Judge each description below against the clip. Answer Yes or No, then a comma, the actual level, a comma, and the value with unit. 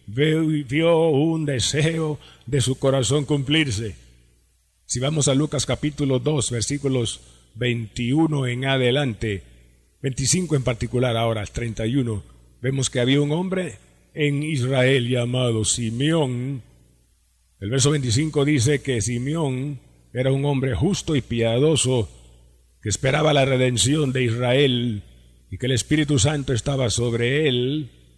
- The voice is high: No, low, 130 Hz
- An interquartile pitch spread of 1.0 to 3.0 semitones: No, average, 4.4 semitones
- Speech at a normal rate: No, slow, 120 wpm